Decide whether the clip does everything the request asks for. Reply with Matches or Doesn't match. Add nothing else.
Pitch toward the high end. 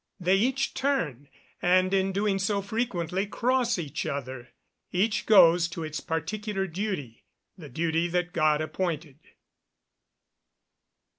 Doesn't match